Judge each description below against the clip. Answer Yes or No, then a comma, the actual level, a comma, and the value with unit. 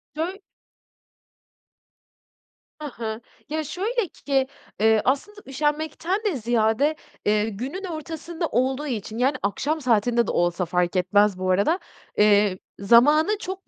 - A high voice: Yes, very high, 260 Hz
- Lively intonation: Yes, wide, 7.0 semitones